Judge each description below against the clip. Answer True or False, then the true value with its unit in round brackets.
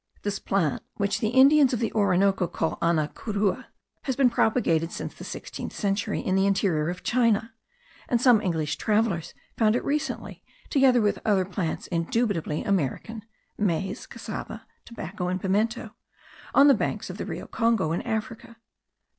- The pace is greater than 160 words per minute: False (155 wpm)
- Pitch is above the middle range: True (205 Hz)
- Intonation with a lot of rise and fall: False (4.4 semitones)